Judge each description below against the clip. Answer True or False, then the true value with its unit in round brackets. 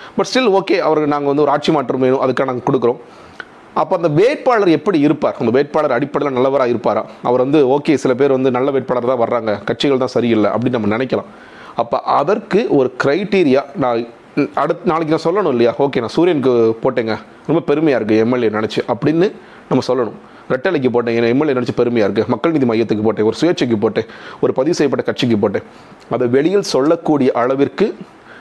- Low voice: True (130 Hz)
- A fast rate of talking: True (175 wpm)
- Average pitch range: True (3.5 semitones)